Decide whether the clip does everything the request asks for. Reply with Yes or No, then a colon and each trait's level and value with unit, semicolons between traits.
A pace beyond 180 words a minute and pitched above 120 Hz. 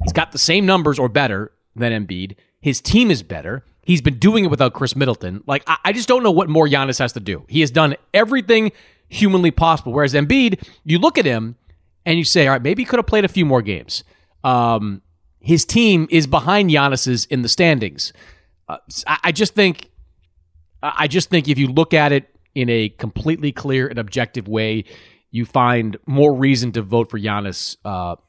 Yes: average, 200 wpm; low, 135 Hz